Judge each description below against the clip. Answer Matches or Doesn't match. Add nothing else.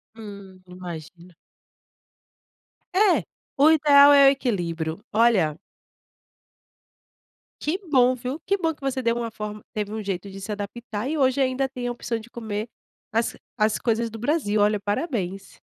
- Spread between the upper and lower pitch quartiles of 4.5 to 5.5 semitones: Matches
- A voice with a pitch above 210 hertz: Matches